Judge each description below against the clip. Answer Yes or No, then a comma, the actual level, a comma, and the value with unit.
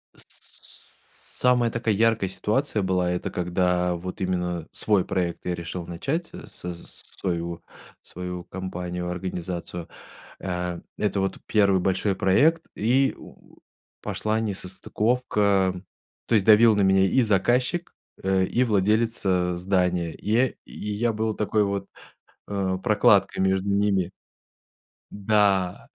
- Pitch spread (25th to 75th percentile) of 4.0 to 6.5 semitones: No, average, 3.1 semitones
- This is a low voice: Yes, very low, 95 Hz